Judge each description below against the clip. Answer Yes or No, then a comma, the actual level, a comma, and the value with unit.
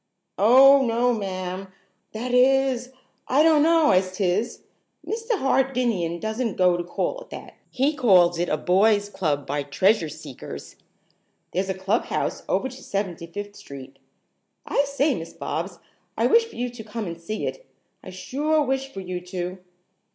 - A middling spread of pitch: No, wide, 6.7 semitones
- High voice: Yes, high, 210 Hz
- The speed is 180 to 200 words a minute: No, average, 160 wpm